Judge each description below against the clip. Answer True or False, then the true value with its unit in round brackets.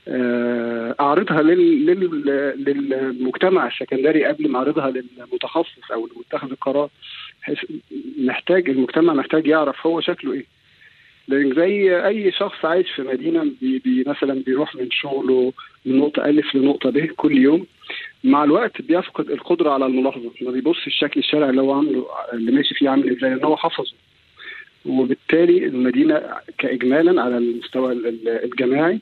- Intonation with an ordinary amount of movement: False (7.0 semitones)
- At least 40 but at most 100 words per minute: False (130 wpm)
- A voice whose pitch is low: False (150 Hz)